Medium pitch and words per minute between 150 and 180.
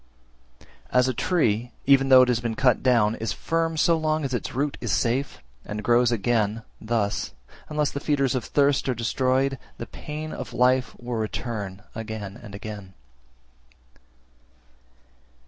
No: low, 125 Hz; average, 155 wpm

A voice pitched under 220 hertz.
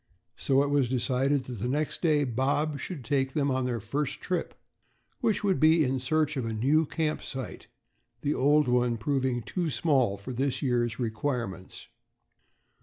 Yes: low, 135 Hz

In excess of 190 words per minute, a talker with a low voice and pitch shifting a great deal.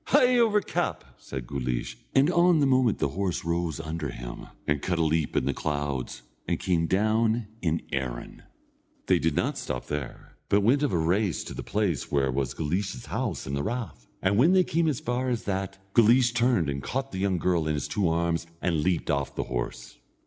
Yes: fast, 205 wpm; very low, 85 Hz; wide, 8.6 semitones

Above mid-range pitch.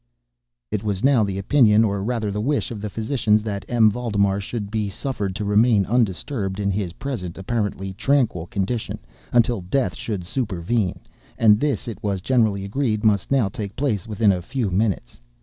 No: low, 105 Hz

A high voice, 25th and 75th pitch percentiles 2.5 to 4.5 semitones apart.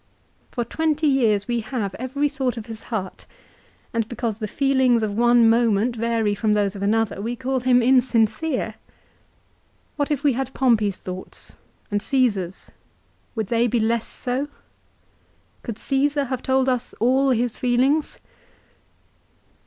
Yes: high, 240 Hz; average, 3.2 semitones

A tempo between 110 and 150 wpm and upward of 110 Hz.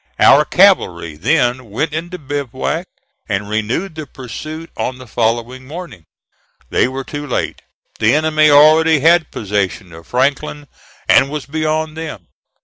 Yes: average, 140 wpm; medium, 140 Hz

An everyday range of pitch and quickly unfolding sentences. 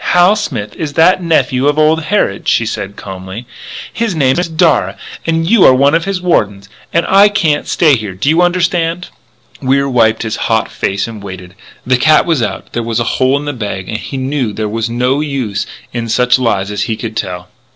No: wide, 6.9 semitones; fast, 210 wpm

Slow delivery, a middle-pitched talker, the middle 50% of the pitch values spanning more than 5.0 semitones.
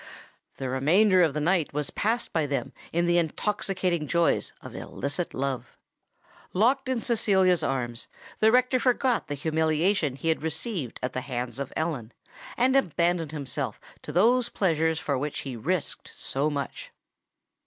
No: average, 155 wpm; medium, 160 Hz; wide, 5.5 semitones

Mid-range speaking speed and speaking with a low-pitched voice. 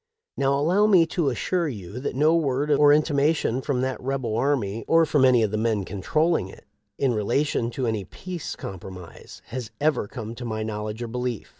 Yes: average, 190 wpm; low, 130 Hz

